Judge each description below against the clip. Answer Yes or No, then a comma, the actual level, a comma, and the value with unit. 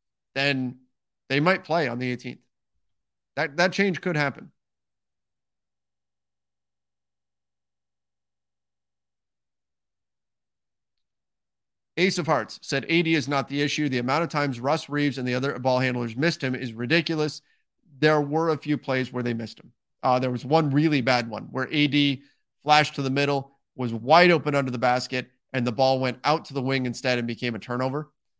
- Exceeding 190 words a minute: No, average, 165 wpm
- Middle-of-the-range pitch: No, low, 130 Hz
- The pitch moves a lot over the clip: No, average, 3.8 semitones